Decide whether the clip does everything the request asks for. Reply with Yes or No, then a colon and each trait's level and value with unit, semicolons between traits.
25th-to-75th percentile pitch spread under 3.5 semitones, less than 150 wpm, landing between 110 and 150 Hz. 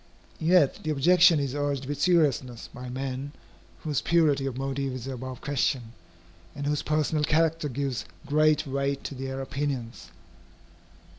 Yes: narrow, 2.4 semitones; average, 140 wpm; medium, 140 Hz